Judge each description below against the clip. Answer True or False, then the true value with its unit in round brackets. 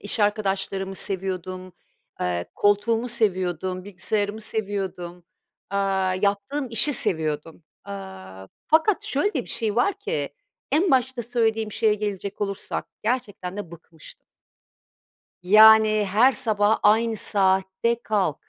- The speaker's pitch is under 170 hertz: False (205 Hz)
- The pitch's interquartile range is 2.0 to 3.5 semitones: True (3.1 semitones)